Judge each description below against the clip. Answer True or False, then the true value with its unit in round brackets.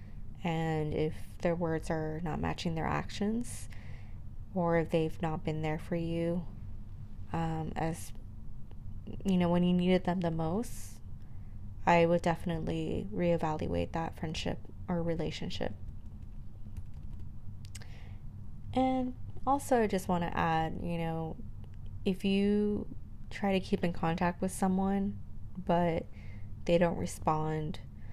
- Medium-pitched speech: True (155 Hz)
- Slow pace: True (120 wpm)